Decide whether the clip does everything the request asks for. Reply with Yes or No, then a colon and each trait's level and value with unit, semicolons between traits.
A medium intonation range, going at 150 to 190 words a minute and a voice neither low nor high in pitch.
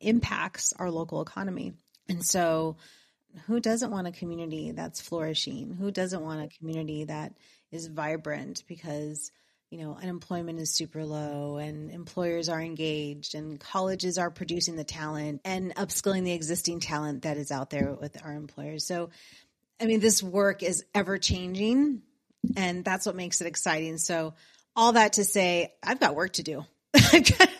Yes: average, 3.6 semitones; average, 160 wpm; medium, 170 Hz